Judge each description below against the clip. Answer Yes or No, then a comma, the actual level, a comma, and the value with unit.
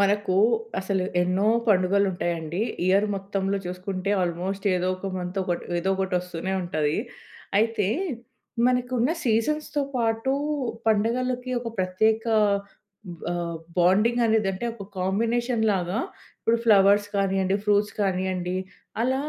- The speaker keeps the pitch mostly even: No, average, 3.5 semitones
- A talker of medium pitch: No, high, 195 Hz